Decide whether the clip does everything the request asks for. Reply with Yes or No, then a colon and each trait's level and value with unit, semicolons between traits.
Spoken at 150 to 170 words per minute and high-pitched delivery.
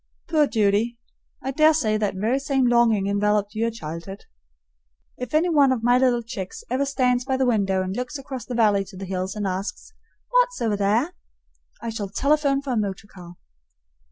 No: average, 185 wpm; high, 230 Hz